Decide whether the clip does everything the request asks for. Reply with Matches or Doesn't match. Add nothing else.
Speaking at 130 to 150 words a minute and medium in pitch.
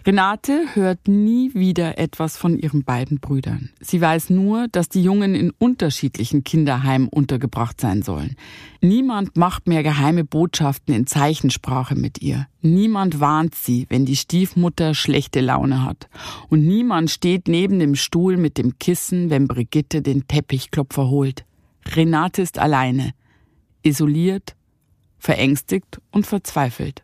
Matches